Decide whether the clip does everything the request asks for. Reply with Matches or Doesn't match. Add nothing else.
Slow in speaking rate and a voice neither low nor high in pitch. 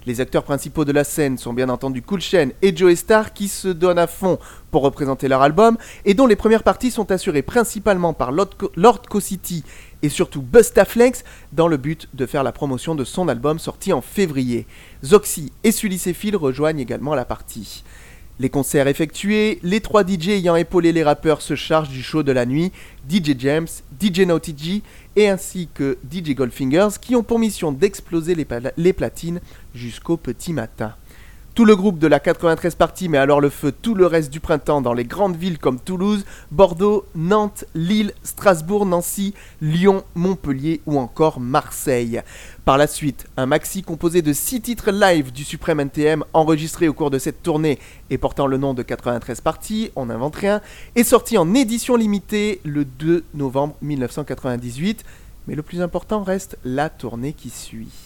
Doesn't match